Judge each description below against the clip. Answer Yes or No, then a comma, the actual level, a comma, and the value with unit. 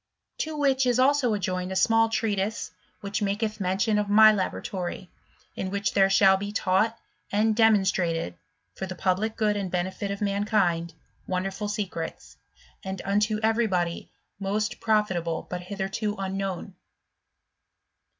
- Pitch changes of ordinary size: No, narrow, 2.3 semitones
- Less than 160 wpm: Yes, average, 140 wpm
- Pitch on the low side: No, high, 200 Hz